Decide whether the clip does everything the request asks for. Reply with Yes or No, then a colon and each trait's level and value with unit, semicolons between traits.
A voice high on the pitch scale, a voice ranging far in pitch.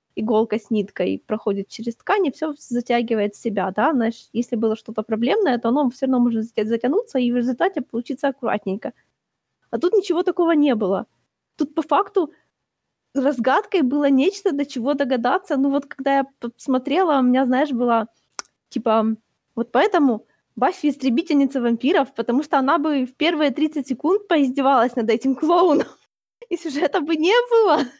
No: very high, 270 Hz; average, 4.8 semitones